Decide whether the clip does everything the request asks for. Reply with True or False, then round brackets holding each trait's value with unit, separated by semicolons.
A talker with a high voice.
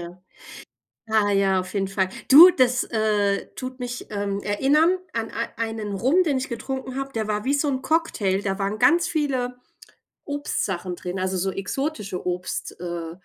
True (220 Hz)